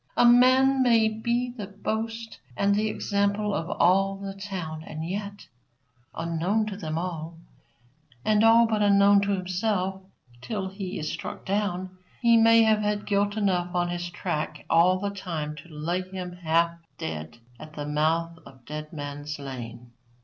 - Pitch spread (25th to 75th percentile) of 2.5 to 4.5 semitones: Yes, average, 4.2 semitones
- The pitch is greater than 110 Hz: Yes, high, 190 Hz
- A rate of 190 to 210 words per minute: No, average, 160 wpm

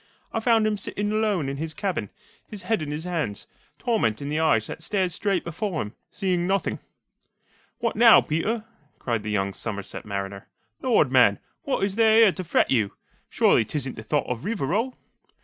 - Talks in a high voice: No, medium, 175 Hz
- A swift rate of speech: No, average, 185 wpm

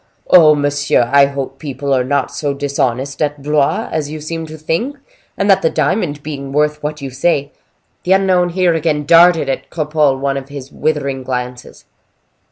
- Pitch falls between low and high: Yes, medium, 145 Hz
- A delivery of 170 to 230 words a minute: Yes, average, 175 wpm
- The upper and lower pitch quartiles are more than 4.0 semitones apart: No, narrow, 2.5 semitones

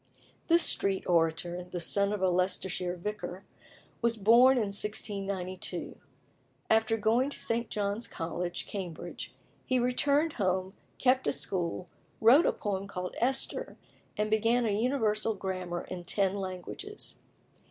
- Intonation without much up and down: No, average, 4.1 semitones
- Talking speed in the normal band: No, slow, 130 wpm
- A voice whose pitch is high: Yes, high, 200 Hz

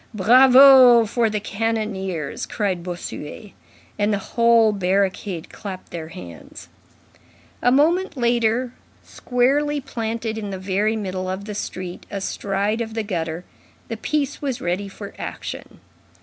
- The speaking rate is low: Yes, slow, 130 wpm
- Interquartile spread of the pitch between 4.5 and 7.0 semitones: No, average, 4.0 semitones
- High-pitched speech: Yes, high, 215 Hz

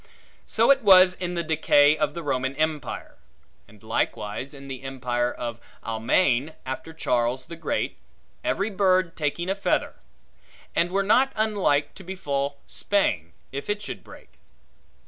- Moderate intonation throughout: No, wide, 6.1 semitones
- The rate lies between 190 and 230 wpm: No, average, 150 wpm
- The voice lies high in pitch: No, medium, 155 Hz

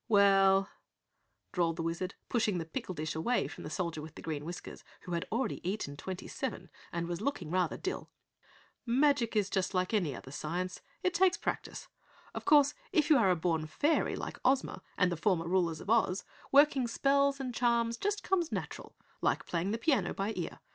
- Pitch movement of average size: No, wide, 6.9 semitones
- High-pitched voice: Yes, high, 195 Hz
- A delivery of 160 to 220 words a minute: Yes, average, 190 wpm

